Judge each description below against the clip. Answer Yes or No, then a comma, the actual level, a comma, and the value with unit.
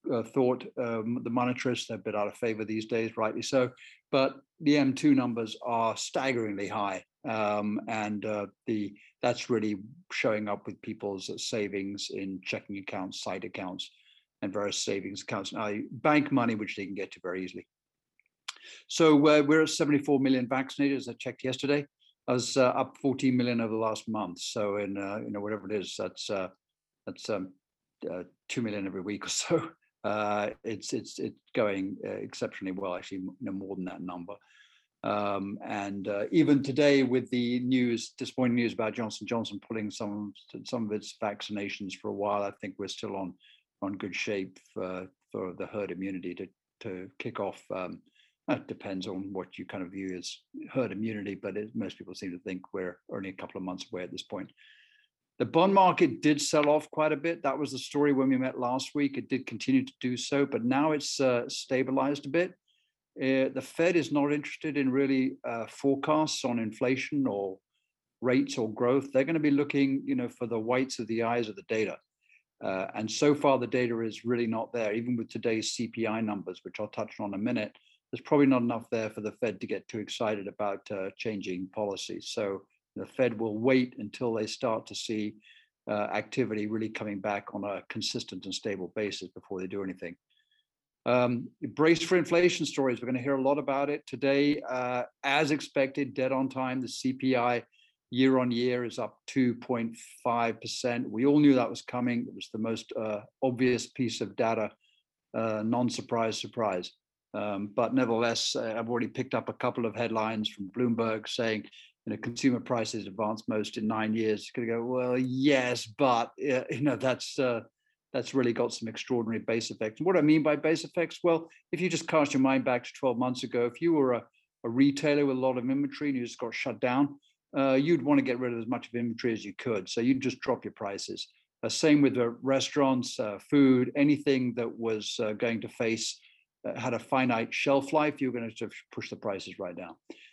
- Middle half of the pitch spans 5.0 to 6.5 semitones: No, average, 4.2 semitones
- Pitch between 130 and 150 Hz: No, low, 120 Hz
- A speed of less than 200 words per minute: No, fast, 205 wpm